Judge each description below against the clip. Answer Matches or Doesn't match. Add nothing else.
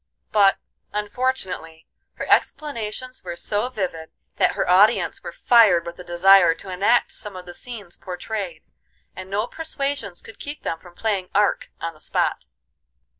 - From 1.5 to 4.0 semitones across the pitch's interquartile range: Doesn't match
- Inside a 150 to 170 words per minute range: Matches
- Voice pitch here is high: Matches